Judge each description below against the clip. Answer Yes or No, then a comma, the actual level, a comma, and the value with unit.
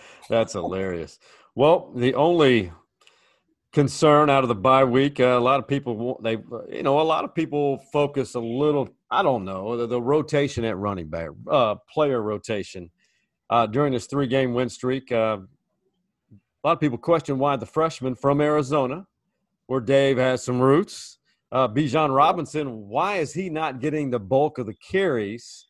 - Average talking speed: Yes, average, 175 wpm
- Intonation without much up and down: No, average, 4.1 semitones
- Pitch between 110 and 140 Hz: Yes, low, 135 Hz